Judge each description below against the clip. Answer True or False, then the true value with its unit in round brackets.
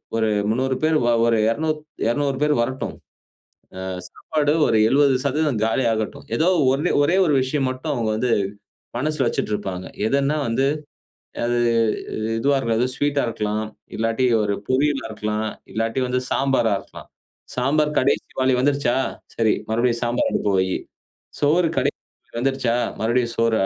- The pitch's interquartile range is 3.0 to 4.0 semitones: True (3.7 semitones)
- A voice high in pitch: False (125 Hz)